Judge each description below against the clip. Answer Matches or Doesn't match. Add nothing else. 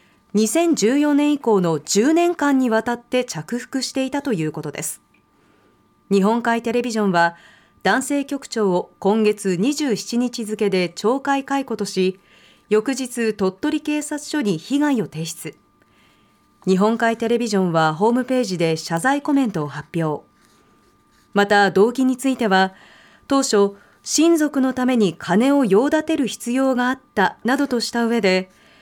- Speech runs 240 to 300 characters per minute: Matches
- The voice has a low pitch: Doesn't match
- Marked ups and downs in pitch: Matches